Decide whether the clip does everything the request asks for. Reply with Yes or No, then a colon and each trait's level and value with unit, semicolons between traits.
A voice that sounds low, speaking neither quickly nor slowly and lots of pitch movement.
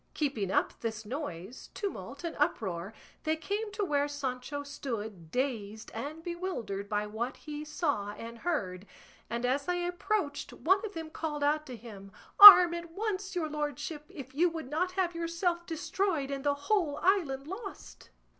No: very high, 295 Hz; average, 165 wpm; wide, 6.4 semitones